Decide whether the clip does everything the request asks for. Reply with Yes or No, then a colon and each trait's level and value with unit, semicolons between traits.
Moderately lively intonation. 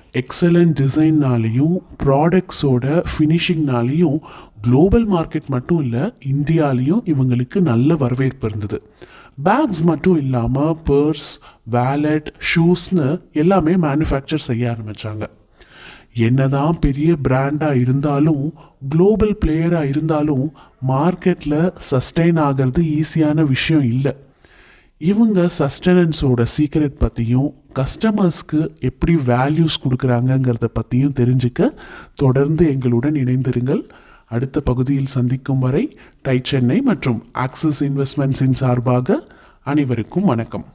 Yes: average, 4.1 semitones